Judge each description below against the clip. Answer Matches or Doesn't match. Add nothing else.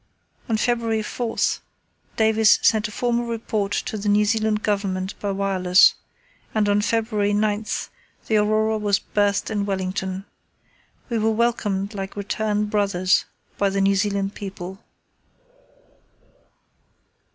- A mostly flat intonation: Matches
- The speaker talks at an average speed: Doesn't match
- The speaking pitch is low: Doesn't match